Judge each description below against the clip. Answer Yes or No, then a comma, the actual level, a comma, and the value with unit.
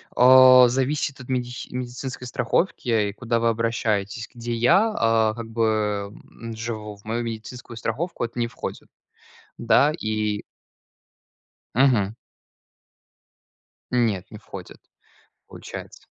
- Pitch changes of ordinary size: No, narrow, 2.0 semitones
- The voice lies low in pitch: Yes, low, 115 Hz